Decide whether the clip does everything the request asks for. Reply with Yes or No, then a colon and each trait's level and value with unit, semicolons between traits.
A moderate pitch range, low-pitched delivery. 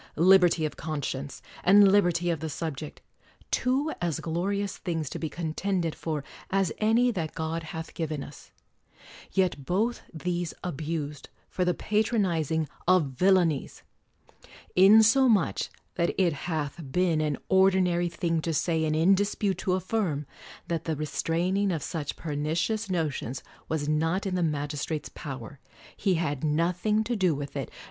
No: average, 3.6 semitones; medium, 170 Hz